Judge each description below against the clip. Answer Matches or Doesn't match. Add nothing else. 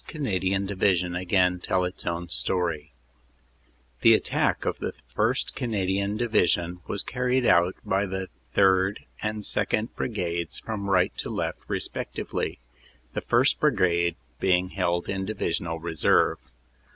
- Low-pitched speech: Matches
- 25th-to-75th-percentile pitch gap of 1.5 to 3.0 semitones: Matches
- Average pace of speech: Doesn't match